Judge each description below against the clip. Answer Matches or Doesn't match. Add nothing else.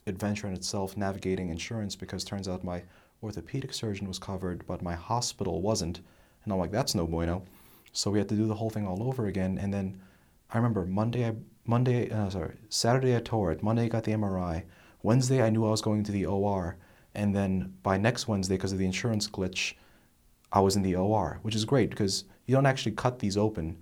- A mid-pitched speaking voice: Doesn't match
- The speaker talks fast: Matches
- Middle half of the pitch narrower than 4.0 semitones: Matches